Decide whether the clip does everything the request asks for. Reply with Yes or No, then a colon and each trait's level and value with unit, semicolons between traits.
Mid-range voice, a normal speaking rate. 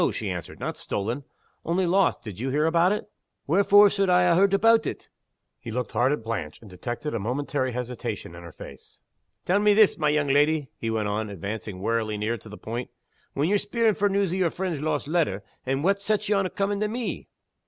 No: medium, 150 Hz; fast, 215 wpm